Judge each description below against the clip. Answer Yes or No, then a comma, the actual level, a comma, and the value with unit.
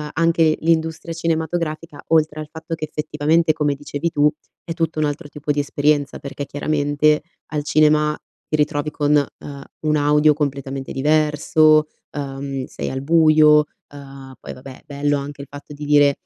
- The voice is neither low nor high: Yes, medium, 150 Hz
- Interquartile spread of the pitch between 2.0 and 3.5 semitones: No, narrow, 1.4 semitones